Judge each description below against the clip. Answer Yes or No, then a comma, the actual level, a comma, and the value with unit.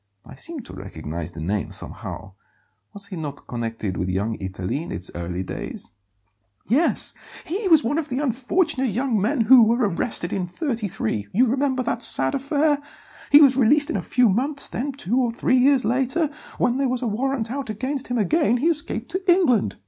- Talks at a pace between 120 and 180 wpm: No, average, 190 wpm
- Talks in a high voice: Yes, high, 245 Hz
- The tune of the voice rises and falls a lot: Yes, wide, 8.4 semitones